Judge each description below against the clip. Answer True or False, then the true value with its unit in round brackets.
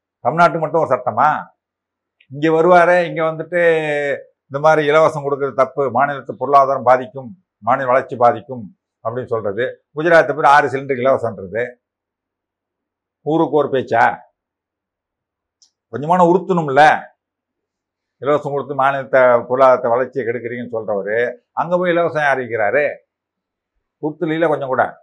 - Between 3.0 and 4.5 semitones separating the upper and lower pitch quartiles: False (5.1 semitones)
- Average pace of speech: True (110 wpm)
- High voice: False (140 Hz)